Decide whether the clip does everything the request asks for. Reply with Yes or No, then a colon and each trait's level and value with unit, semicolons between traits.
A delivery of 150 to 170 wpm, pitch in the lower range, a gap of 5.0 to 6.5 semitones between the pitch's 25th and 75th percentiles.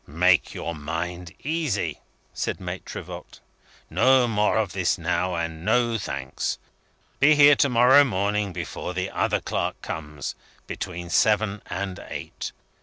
No: slow, 135 wpm; very low, 95 Hz; average, 5.3 semitones